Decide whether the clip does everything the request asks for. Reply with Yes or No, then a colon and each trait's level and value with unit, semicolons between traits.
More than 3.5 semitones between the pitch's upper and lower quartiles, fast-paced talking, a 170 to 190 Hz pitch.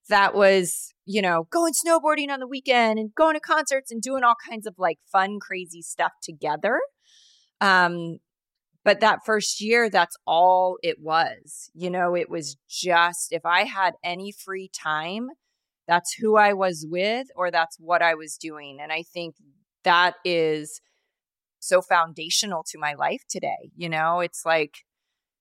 No: average, 5.1 semitones; average, 165 wpm; medium, 185 Hz